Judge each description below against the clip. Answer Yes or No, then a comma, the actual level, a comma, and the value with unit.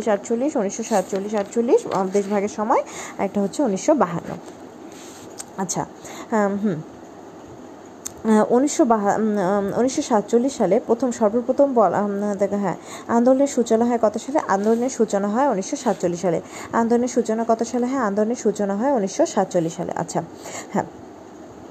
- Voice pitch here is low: No, high, 220 Hz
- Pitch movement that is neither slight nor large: Yes, average, 3.4 semitones